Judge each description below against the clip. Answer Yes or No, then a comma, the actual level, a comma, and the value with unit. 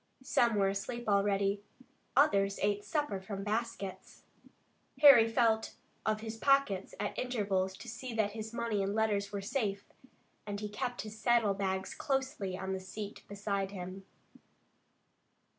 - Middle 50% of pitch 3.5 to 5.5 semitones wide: No, average, 2.9 semitones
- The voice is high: Yes, high, 205 Hz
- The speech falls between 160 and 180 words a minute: No, average, 145 wpm